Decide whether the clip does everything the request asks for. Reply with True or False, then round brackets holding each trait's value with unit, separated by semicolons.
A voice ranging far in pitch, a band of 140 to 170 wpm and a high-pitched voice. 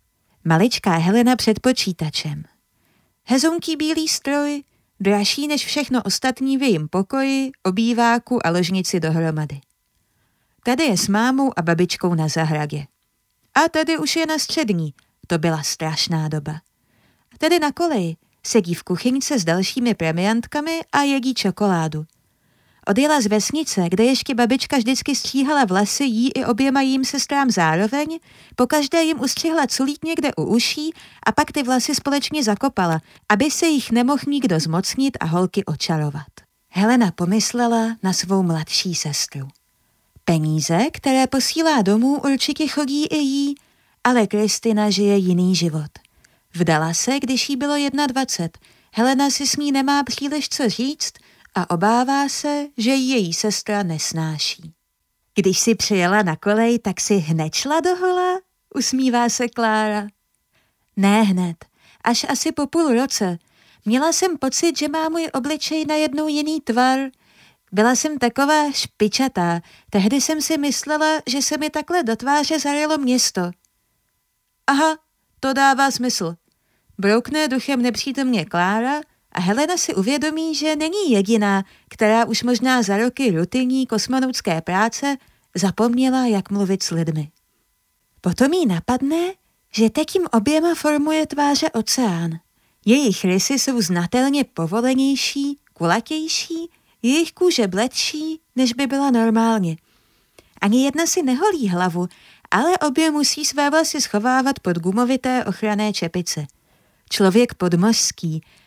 False (7.2 semitones; 130 wpm; 245 Hz)